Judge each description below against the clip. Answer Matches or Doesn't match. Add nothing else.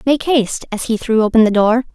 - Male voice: Doesn't match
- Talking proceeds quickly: Matches